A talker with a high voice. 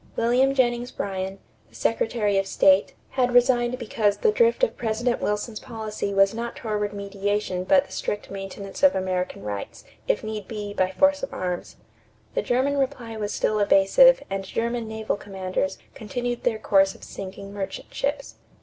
Yes: high, 215 Hz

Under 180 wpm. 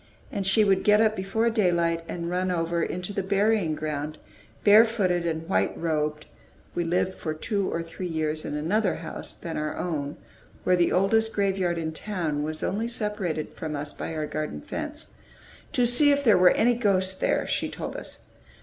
No: average, 185 wpm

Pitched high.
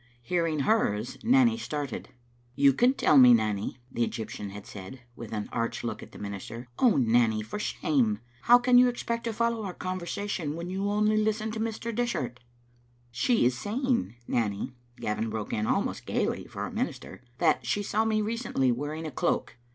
No: medium, 150 Hz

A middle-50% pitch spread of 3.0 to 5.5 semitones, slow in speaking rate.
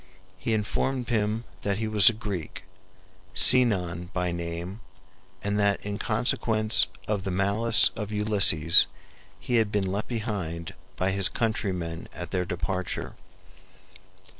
Yes: average, 3.3 semitones; slow, 130 wpm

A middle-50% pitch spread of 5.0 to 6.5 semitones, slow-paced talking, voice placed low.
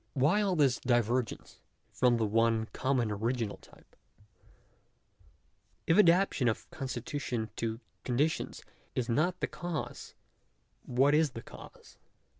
No: average, 4.5 semitones; slow, 115 wpm; low, 125 Hz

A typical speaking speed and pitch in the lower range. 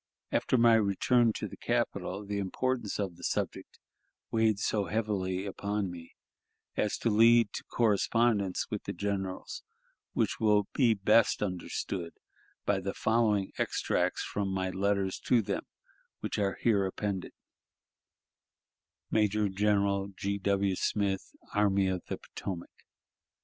No: slow, 130 wpm; low, 100 Hz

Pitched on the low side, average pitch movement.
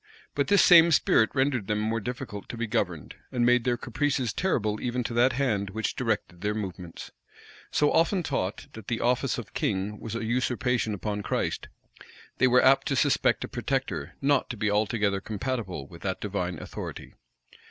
Yes: low, 115 Hz; average, 3.9 semitones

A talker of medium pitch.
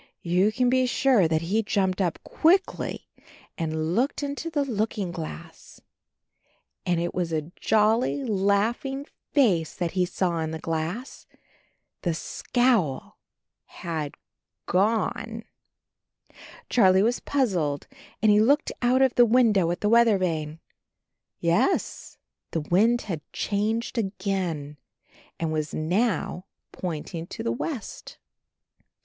No: high, 195 Hz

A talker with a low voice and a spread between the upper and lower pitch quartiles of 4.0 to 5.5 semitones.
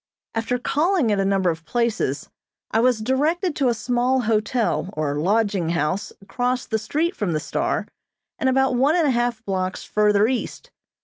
No: high, 230 Hz; average, 4.7 semitones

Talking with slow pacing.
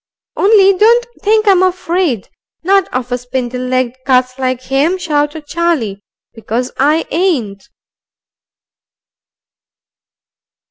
Yes: slow, 100 wpm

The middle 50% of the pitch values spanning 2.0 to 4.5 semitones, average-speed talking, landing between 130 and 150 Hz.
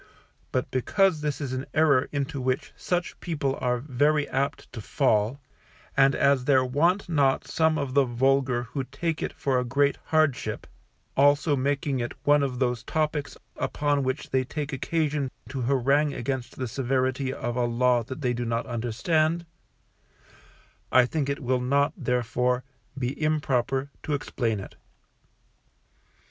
Yes: narrow, 2.6 semitones; average, 155 wpm; low, 135 Hz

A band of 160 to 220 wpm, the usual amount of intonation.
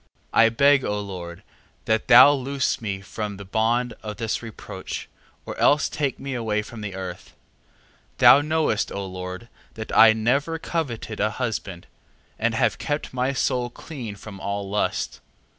Yes: average, 165 wpm; average, 4.3 semitones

